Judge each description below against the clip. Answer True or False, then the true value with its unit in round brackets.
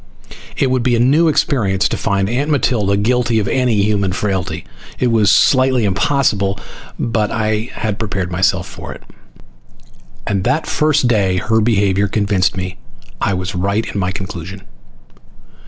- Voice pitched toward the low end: True (105 Hz)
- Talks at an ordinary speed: True (155 wpm)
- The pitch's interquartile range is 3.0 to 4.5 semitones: True (3.9 semitones)